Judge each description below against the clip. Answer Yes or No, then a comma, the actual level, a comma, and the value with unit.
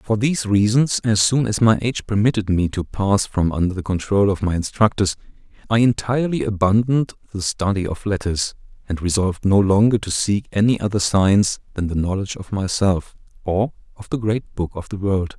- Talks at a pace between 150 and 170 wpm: No, average, 185 wpm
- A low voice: Yes, low, 100 Hz